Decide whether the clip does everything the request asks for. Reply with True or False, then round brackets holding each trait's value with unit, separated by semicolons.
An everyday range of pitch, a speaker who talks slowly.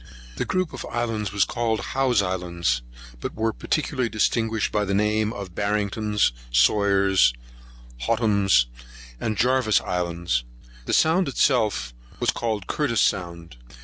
True (3.9 semitones; 125 wpm)